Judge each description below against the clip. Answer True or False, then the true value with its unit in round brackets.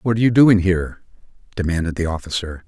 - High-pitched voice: False (90 Hz)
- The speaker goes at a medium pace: True (180 wpm)